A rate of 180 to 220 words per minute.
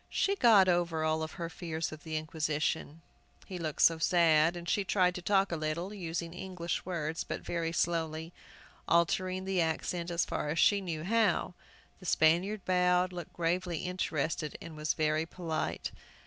No: average, 165 wpm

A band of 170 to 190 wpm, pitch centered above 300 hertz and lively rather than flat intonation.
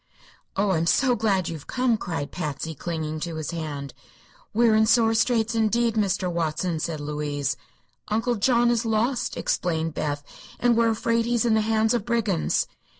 No: average, 175 wpm; high, 210 Hz; wide, 6.2 semitones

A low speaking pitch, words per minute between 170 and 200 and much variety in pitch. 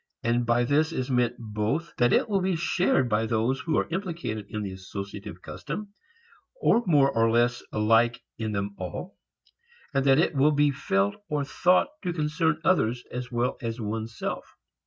Yes: low, 125 Hz; average, 180 wpm; wide, 5.7 semitones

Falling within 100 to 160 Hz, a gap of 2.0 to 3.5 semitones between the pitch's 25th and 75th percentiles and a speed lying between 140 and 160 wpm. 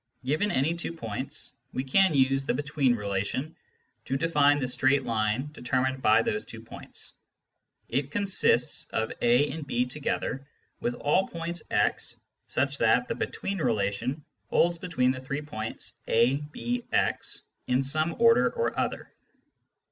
No: low, 135 Hz; average, 4.0 semitones; average, 150 wpm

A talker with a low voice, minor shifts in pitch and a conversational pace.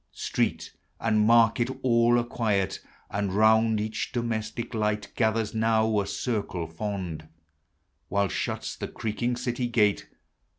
No: low, 110 Hz; narrow, 2.2 semitones; slow, 125 wpm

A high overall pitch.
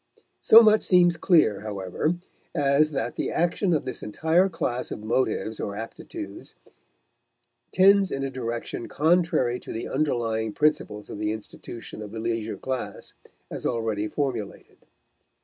No: low, 130 Hz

